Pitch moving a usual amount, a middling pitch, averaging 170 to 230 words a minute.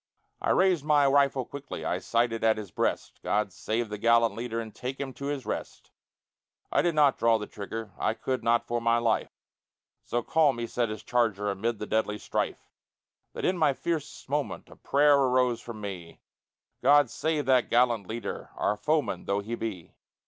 No: average, 4.1 semitones; low, 120 Hz; average, 185 wpm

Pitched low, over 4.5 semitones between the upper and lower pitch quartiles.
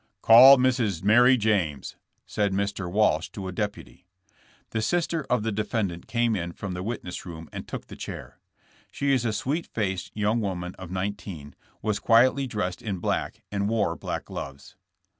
No: low, 105 Hz; average, 4.0 semitones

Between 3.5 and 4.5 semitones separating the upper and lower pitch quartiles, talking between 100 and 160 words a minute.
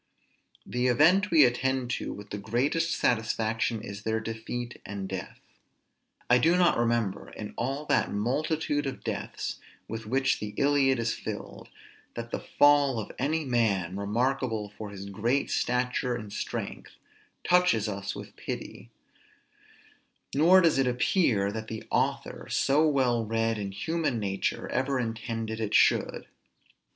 Yes: average, 4.1 semitones; average, 140 wpm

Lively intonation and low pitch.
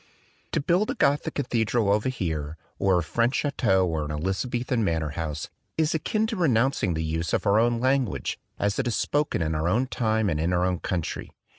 Yes: wide, 7.7 semitones; low, 105 Hz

